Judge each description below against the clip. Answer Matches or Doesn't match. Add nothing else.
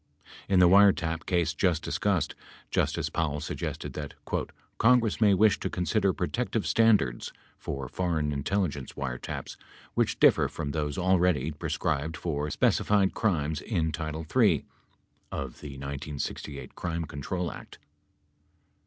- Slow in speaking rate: Matches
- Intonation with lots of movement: Doesn't match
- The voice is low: Matches